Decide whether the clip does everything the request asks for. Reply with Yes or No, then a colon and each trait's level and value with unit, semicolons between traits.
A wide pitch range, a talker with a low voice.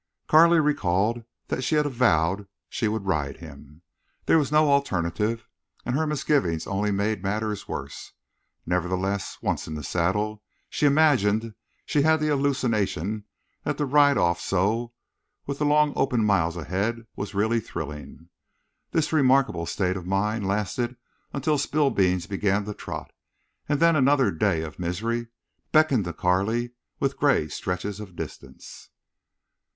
Yes: wide, 6.9 semitones; low, 105 Hz